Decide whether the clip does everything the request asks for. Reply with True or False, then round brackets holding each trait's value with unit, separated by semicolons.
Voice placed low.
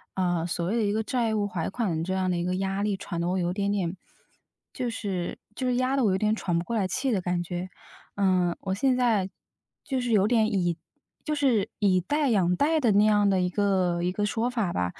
False (200 Hz)